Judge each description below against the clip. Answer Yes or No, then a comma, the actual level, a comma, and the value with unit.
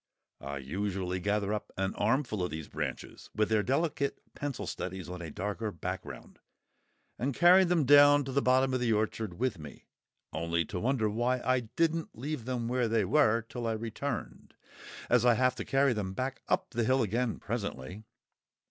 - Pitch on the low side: Yes, low, 115 Hz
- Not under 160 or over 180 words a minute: Yes, average, 175 wpm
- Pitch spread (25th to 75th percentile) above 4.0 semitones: Yes, average, 4.7 semitones